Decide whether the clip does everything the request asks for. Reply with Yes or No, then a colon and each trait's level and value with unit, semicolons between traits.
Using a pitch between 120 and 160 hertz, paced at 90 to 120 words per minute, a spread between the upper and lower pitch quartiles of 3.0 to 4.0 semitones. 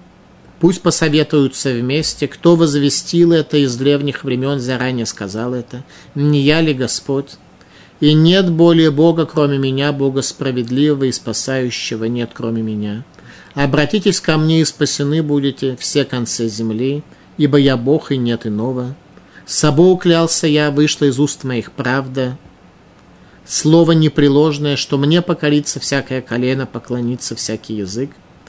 No: medium, 140 Hz; average, 135 wpm; average, 3.7 semitones